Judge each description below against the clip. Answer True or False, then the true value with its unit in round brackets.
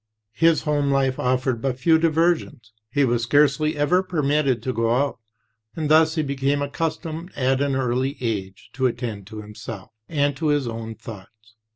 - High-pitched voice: False (135 Hz)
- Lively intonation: False (4.3 semitones)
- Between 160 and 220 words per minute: True (170 wpm)